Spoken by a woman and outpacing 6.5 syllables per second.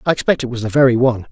No: male; 8.5 syllables/s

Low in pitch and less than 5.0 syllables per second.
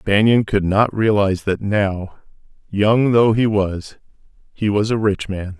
Yes: low, 105 Hz; 4.0 syllables/s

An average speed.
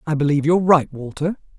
Yes: average, 190 wpm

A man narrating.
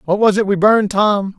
Yes: male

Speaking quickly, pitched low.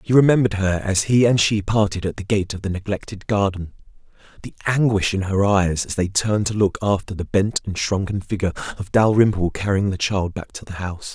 Yes: fast, 215 wpm; low, 100 Hz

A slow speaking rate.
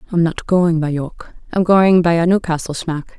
No: fast, 205 wpm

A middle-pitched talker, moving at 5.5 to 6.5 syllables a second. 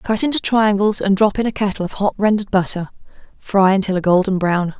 No: high, 200 Hz; 5.9 syllables/s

